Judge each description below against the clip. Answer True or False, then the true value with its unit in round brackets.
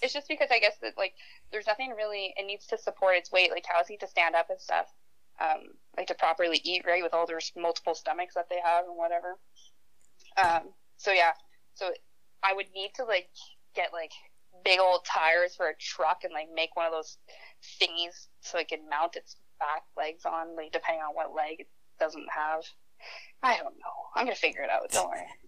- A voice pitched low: False (175 Hz)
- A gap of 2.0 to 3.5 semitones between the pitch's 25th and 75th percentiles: True (2.9 semitones)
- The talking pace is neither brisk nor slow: False (210 wpm)